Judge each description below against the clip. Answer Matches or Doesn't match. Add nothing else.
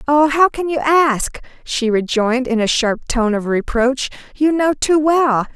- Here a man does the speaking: Doesn't match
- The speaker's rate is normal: Matches